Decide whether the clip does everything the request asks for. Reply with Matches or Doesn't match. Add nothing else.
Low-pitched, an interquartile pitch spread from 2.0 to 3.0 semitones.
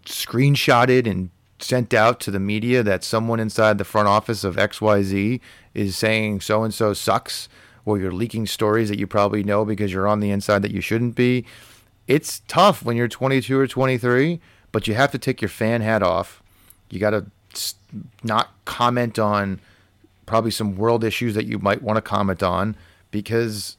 Matches